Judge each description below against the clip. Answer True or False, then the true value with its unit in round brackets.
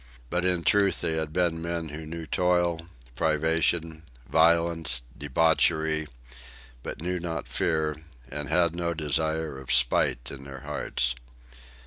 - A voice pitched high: False (80 Hz)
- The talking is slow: True (130 wpm)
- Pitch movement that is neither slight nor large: False (1.9 semitones)